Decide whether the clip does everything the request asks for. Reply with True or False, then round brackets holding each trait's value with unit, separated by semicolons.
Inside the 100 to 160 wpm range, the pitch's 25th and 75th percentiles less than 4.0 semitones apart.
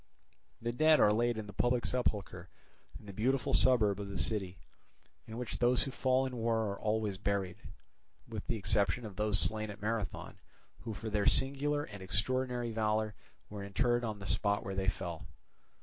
False (180 wpm; 3.1 semitones)